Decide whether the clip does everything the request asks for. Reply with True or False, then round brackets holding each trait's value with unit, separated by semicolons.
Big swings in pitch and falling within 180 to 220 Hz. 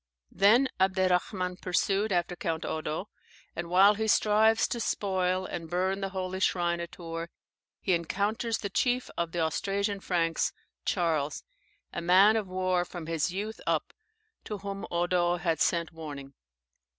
False (2.7 semitones; 185 Hz)